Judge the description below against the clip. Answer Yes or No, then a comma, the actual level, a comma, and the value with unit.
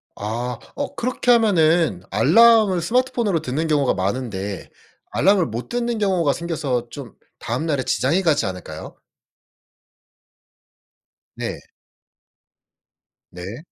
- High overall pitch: No, medium, 155 Hz